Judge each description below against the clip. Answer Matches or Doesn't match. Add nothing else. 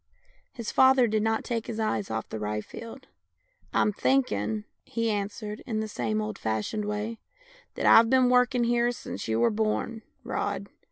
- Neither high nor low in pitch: Doesn't match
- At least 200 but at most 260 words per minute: Doesn't match